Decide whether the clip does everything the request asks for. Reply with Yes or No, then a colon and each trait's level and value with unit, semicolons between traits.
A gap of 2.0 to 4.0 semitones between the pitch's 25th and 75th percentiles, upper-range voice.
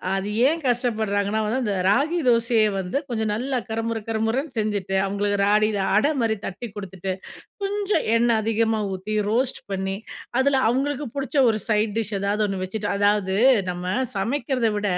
Yes: average, 3.2 semitones; high, 220 Hz